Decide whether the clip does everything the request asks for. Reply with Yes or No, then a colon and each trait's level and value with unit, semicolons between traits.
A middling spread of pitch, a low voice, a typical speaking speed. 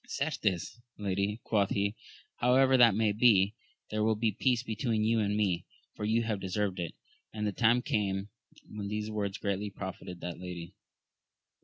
No: narrow, 2.3 semitones; low, 105 Hz; average, 165 wpm